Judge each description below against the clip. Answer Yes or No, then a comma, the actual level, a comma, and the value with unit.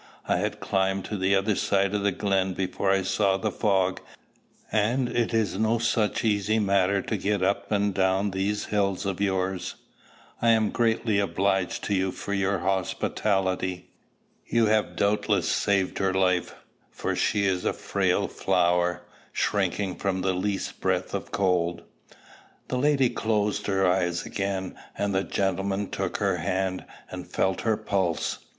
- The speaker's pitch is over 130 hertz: No, very low, 95 Hz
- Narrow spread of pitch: Yes, narrow, 1.6 semitones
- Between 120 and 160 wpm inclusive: Yes, average, 155 wpm